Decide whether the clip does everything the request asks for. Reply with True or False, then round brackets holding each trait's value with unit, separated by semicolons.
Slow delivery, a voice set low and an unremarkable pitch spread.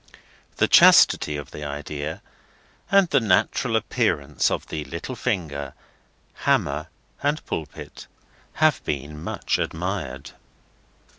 True (105 wpm; 75 Hz; 4.4 semitones)